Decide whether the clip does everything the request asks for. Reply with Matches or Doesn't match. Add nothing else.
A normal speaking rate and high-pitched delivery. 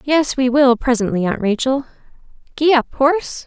Matches